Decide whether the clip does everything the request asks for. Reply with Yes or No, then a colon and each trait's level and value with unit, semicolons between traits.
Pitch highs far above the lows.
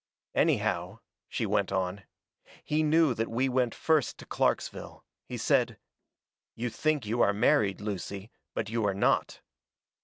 No: average, 4.6 semitones